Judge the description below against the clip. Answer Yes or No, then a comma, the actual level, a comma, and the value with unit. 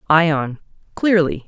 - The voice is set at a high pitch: No, medium, 160 Hz